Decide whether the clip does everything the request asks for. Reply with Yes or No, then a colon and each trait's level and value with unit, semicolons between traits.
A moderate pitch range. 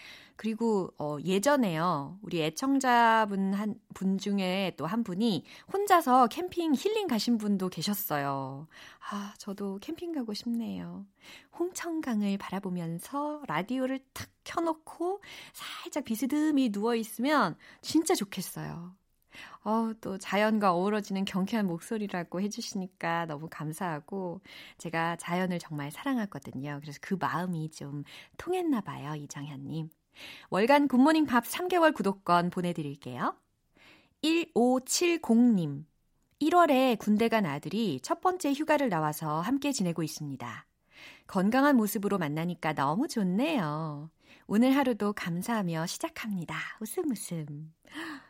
No: wide, 7.8 semitones